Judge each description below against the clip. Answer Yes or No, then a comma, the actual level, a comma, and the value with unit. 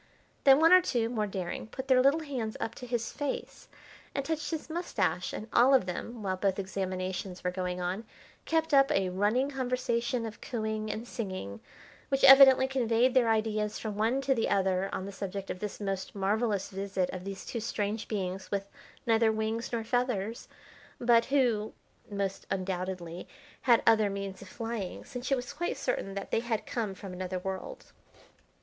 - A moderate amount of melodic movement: Yes, average, 4.4 semitones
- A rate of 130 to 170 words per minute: No, average, 180 wpm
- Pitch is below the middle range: No, high, 220 Hz